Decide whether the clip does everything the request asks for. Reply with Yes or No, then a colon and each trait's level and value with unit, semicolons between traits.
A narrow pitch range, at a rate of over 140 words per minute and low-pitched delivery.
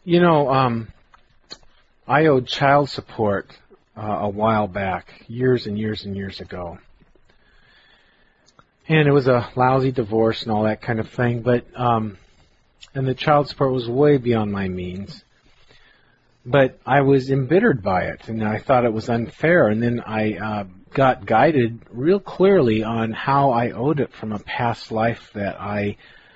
No: average, 4.1 semitones; average, 160 wpm; low, 115 Hz